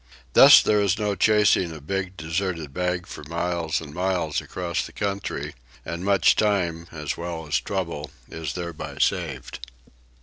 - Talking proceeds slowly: No, average, 155 wpm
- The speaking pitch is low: Yes, very low, 85 Hz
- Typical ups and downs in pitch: Yes, average, 3.0 semitones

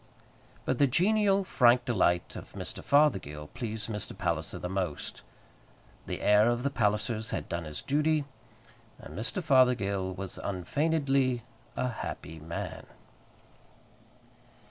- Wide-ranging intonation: Yes, wide, 6.6 semitones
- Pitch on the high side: No, low, 120 Hz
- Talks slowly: Yes, slow, 120 wpm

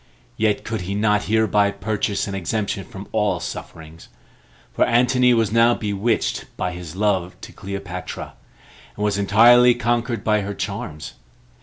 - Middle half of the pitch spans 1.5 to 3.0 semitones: Yes, average, 2.7 semitones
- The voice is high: No, low, 105 Hz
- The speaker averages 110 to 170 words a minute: Yes, average, 145 wpm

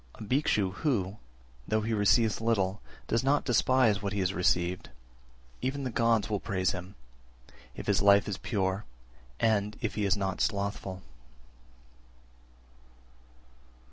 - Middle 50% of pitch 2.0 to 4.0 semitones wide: Yes, average, 2.9 semitones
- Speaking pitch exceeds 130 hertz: No, low, 105 Hz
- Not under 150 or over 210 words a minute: No, average, 140 wpm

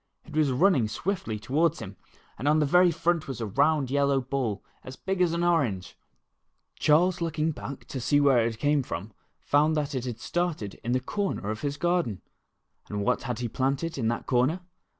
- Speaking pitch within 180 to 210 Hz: No, medium, 140 Hz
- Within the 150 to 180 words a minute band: No, average, 195 wpm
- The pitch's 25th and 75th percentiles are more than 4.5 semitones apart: Yes, wide, 5.4 semitones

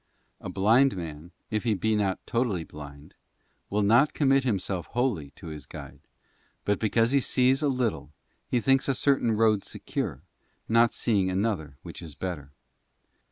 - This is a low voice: Yes, low, 110 Hz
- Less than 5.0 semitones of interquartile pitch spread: No, wide, 5.6 semitones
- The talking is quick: No, average, 160 wpm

